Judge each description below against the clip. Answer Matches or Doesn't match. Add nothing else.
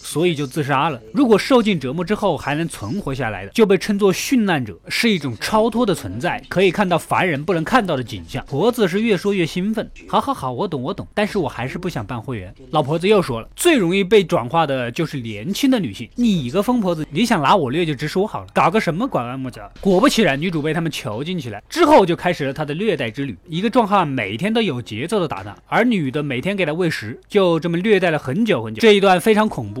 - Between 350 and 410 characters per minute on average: Matches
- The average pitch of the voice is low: Doesn't match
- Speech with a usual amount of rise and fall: Doesn't match